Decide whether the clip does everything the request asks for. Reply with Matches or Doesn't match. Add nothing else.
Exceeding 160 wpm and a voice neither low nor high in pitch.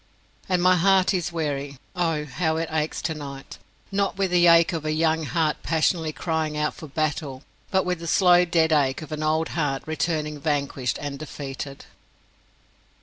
Matches